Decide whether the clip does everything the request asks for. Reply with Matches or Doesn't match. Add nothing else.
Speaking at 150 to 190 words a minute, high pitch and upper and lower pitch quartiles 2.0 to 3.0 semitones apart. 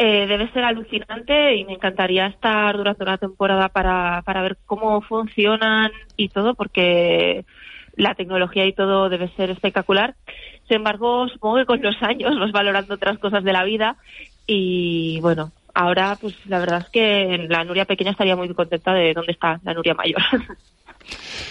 Matches